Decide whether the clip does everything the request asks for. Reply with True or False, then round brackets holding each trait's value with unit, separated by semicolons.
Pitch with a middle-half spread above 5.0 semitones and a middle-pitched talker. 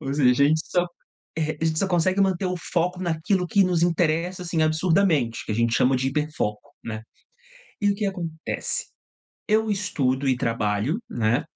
True (5.5 semitones; 160 Hz)